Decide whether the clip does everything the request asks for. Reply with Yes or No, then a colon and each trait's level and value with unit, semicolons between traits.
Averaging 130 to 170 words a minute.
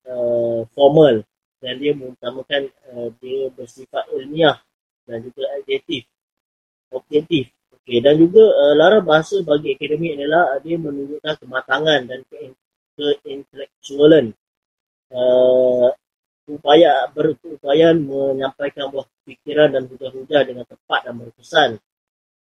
No: average, 110 wpm